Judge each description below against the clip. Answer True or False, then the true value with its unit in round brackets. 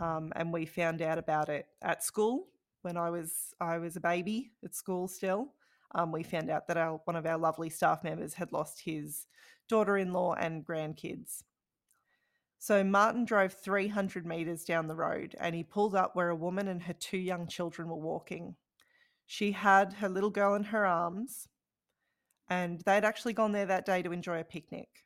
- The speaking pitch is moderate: True (180 Hz)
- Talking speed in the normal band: True (190 wpm)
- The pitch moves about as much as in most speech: True (3.3 semitones)